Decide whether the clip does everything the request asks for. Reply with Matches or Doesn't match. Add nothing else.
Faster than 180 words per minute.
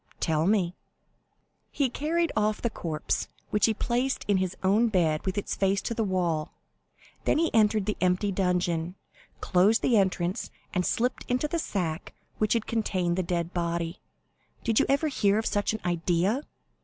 Doesn't match